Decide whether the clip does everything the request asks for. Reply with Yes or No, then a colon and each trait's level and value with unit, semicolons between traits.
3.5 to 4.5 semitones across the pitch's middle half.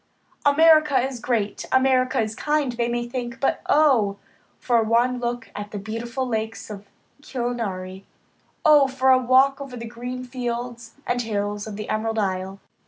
No: average, 3.0 semitones